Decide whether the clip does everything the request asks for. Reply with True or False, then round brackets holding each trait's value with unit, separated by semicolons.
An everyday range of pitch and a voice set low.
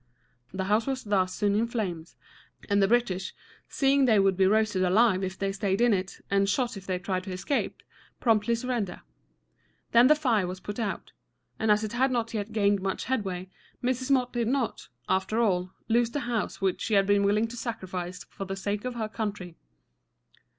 False (3.7 semitones; 210 Hz)